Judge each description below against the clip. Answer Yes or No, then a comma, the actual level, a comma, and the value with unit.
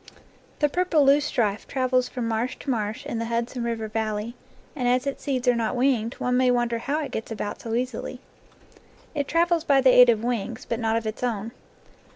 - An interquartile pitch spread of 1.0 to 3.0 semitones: Yes, narrow, 2.6 semitones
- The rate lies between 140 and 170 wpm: No, average, 200 wpm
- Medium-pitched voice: No, high, 245 Hz